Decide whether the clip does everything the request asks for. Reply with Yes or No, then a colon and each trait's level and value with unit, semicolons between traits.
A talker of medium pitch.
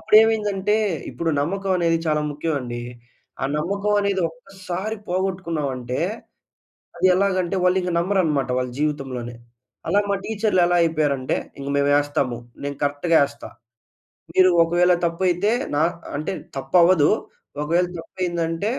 Yes: medium, 170 Hz